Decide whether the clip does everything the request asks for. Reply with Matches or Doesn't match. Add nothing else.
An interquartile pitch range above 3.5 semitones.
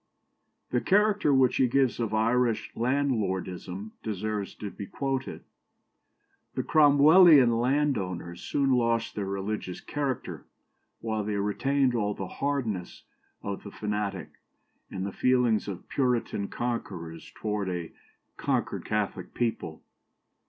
Matches